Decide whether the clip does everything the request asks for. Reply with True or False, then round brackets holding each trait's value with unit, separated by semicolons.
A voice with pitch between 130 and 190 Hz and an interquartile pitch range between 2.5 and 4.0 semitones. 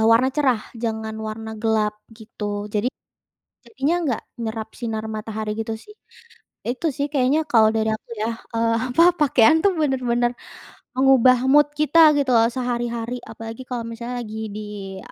False (235 Hz; 3.2 semitones)